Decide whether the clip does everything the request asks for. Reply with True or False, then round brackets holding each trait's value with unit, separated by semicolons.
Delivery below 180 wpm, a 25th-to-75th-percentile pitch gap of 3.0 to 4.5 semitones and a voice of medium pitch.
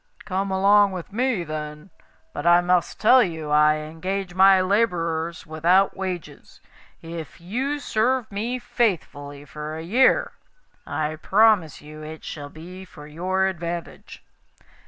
True (135 wpm; 4.0 semitones; 175 Hz)